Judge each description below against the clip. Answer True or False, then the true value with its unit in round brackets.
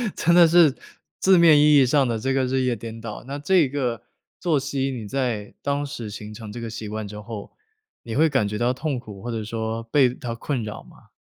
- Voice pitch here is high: False (125 Hz)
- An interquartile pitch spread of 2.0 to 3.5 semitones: False (4.2 semitones)